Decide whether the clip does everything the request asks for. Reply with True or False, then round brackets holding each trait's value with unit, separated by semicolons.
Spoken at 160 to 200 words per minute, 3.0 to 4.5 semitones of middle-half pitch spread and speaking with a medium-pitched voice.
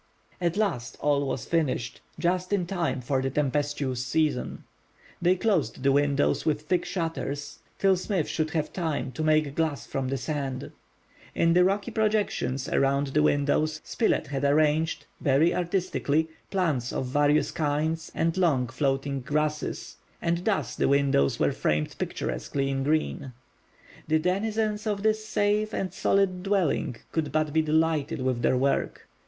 False (150 wpm; 4.2 semitones; 155 Hz)